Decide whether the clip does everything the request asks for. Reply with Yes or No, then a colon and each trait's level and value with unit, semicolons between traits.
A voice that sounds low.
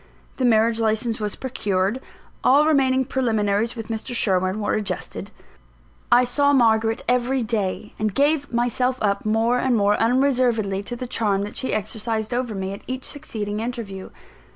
No: high, 225 Hz